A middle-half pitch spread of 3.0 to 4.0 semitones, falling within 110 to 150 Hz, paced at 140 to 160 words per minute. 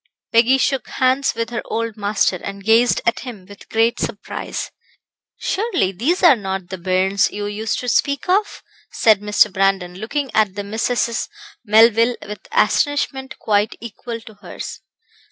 No: average, 3.6 semitones; high, 225 Hz; average, 155 wpm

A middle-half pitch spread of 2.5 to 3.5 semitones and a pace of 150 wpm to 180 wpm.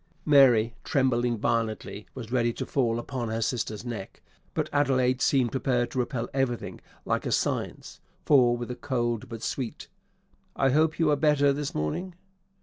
Yes: average, 2.8 semitones; average, 165 wpm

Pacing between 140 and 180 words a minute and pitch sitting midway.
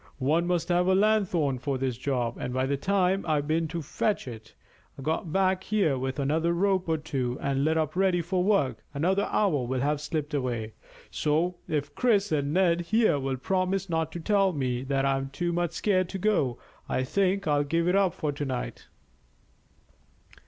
No: average, 190 wpm; medium, 160 Hz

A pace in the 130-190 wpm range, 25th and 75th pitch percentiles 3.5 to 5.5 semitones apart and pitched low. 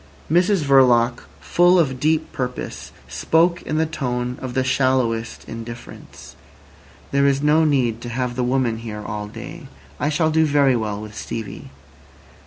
Yes: average, 155 wpm; average, 4.5 semitones; low, 130 Hz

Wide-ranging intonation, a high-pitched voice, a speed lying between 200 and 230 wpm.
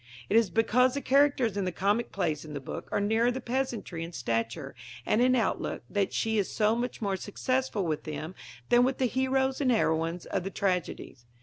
Yes: wide, 6.1 semitones; high, 215 Hz; fast, 205 wpm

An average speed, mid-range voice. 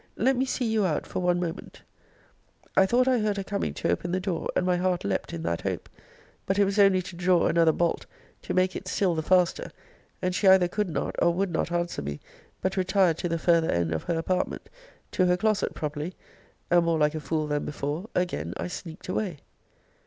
No: fast, 220 wpm; medium, 180 Hz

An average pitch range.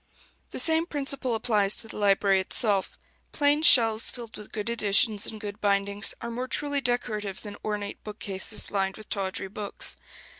Yes: average, 3.3 semitones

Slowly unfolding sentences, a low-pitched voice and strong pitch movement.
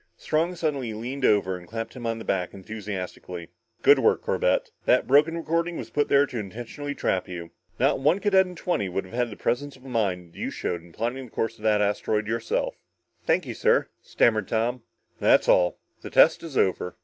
No: average, 200 wpm; low, 115 Hz; wide, 6.1 semitones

